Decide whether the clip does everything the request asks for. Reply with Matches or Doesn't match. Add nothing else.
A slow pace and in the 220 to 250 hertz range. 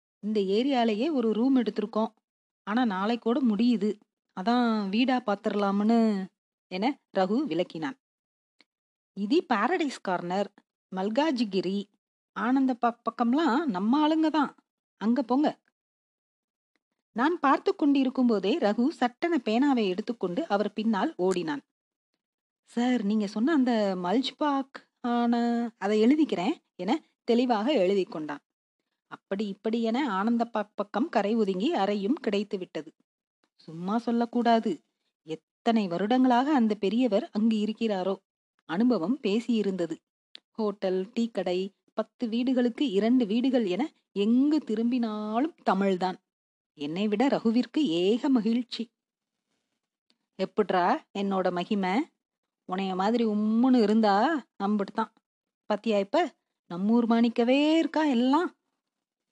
Doesn't match